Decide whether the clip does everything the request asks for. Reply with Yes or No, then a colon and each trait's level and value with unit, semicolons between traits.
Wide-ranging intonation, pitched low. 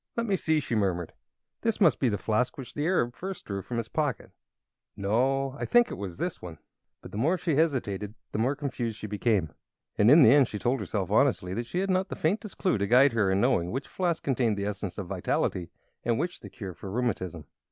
Yes: wide, 6.8 semitones; low, 120 Hz